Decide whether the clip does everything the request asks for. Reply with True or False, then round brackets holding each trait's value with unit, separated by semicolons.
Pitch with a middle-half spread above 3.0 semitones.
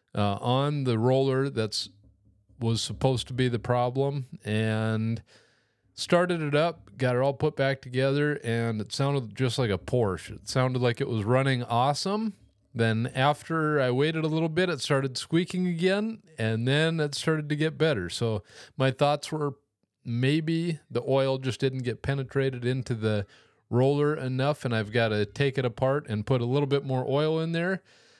True (4.2 semitones)